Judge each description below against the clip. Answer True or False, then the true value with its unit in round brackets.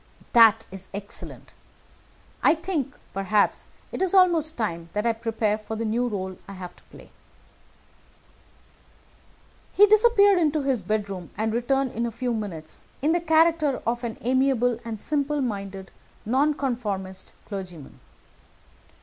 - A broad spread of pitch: True (6.1 semitones)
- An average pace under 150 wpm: True (135 wpm)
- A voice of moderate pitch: False (230 Hz)